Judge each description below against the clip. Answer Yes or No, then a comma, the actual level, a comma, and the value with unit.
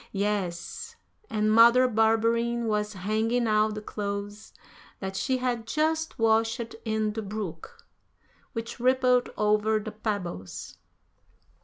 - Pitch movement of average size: No, narrow, 2.1 semitones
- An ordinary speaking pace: No, slow, 115 wpm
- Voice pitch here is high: Yes, high, 220 Hz